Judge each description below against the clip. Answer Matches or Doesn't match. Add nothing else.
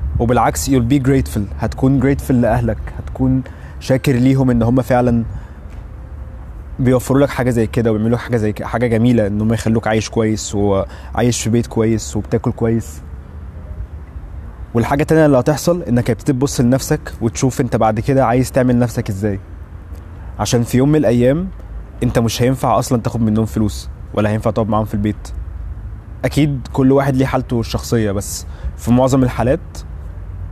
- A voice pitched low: Matches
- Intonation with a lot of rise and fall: Matches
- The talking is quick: Matches